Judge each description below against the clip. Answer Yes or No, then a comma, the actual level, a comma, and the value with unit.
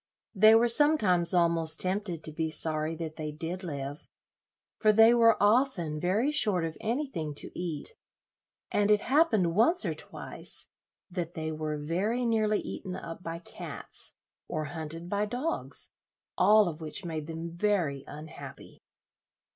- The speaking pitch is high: No, medium, 175 Hz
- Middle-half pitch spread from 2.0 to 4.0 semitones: No, average, 5.2 semitones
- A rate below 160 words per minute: Yes, average, 145 wpm